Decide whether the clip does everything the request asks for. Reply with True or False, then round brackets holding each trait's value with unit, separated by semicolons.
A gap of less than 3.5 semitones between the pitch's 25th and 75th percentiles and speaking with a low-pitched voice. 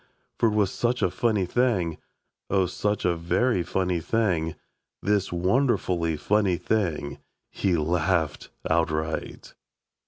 False (4.1 semitones; 90 Hz)